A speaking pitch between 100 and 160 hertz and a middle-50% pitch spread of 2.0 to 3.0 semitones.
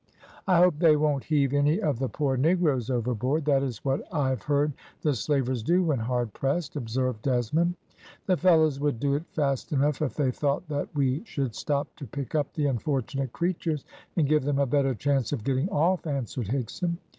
Yes: medium, 140 Hz; average, 2.7 semitones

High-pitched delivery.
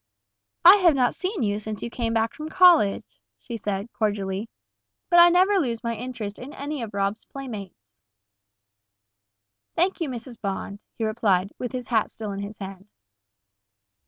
Yes: high, 230 Hz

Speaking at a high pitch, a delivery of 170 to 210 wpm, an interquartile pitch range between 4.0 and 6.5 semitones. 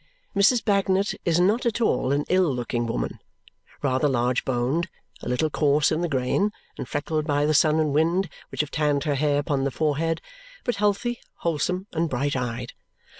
No: medium, 150 Hz; average, 180 wpm; average, 4.6 semitones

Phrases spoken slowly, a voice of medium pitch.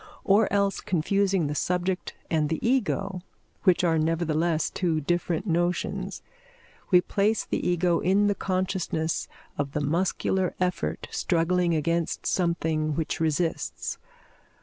Yes: slow, 125 wpm; medium, 175 Hz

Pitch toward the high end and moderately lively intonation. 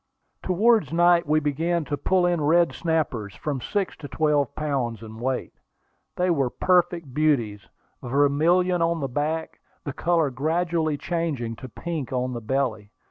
No: medium, 150 Hz; average, 4.5 semitones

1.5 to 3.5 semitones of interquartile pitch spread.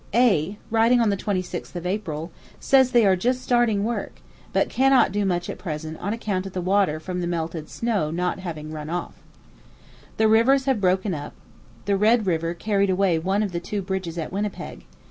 No: average, 4.0 semitones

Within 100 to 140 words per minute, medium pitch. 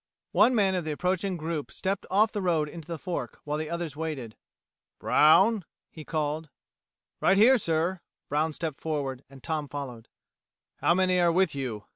No: average, 170 wpm; medium, 160 Hz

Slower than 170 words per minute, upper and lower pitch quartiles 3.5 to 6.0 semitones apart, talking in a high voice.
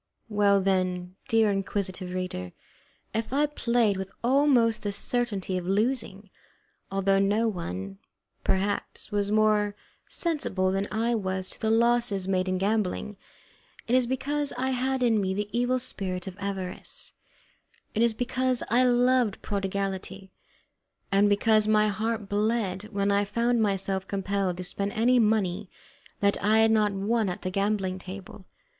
No: average, 150 wpm; average, 3.1 semitones; high, 205 Hz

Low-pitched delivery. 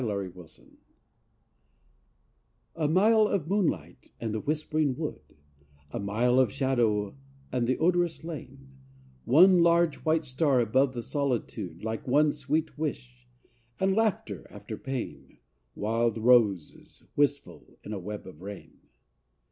Yes: low, 130 Hz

